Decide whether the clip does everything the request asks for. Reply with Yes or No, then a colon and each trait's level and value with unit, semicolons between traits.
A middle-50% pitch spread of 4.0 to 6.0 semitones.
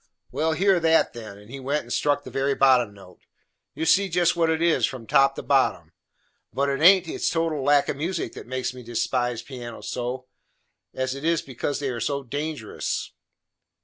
Yes: average, 4.4 semitones